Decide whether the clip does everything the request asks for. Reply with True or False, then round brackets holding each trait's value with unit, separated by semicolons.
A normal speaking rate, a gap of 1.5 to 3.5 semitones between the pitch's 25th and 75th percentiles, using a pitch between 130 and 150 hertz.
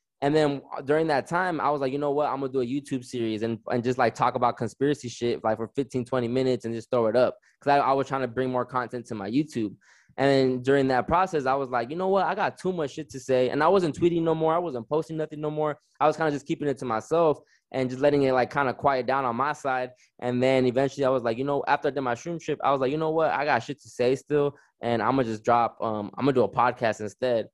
False (295 wpm; 3.2 semitones; 135 Hz)